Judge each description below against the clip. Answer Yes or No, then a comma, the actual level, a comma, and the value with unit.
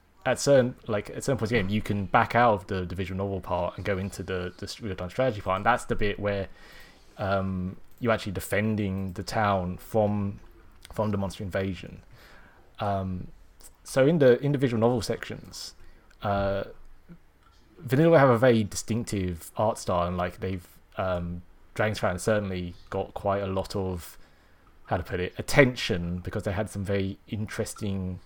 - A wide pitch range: No, average, 3.2 semitones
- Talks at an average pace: Yes, average, 170 wpm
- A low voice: Yes, low, 100 Hz